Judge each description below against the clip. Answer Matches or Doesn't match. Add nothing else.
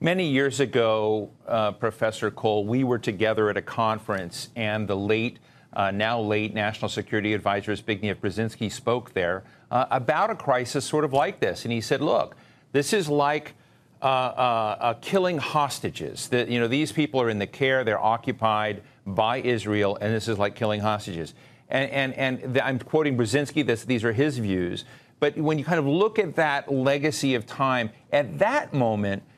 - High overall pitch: Doesn't match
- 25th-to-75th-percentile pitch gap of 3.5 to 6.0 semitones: Matches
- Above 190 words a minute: Doesn't match